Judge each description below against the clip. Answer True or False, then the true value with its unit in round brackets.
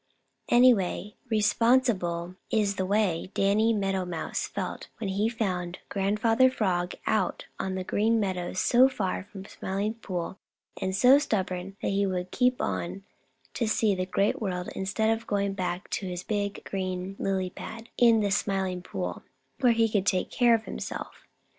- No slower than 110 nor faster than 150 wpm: False (170 wpm)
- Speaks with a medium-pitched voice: False (200 Hz)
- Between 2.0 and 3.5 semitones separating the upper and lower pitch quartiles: True (3.2 semitones)